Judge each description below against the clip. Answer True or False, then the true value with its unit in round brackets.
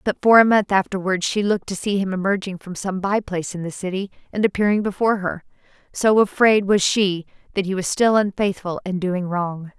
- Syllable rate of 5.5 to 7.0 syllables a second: True (5.6 syllables/s)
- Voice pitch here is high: True (195 Hz)